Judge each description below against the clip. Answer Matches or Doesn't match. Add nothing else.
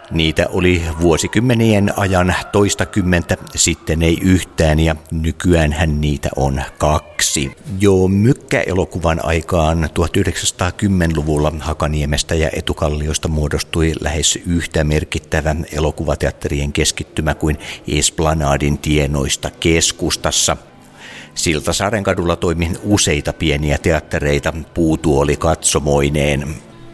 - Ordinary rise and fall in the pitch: Matches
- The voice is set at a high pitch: Doesn't match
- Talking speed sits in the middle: Doesn't match